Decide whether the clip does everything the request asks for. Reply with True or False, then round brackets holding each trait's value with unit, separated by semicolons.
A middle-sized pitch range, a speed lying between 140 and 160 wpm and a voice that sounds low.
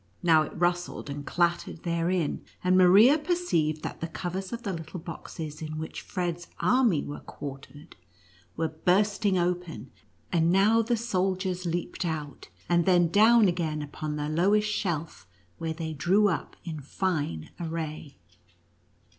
False (3.2 semitones; 145 wpm; 175 Hz)